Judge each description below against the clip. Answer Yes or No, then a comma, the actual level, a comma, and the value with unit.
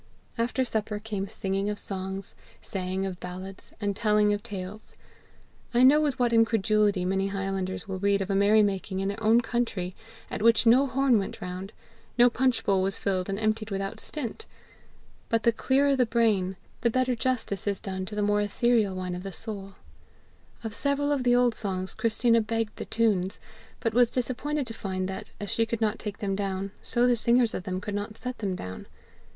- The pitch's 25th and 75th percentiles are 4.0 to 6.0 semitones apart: No, average, 3.2 semitones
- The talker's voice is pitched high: Yes, high, 210 Hz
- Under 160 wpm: No, average, 195 wpm